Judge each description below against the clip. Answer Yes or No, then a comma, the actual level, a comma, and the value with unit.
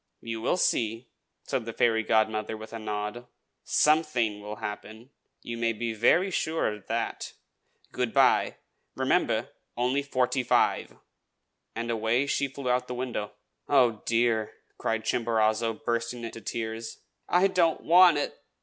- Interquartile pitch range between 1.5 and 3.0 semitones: Yes, narrow, 2.5 semitones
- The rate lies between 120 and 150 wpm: Yes, average, 145 wpm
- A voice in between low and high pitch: No, low, 115 Hz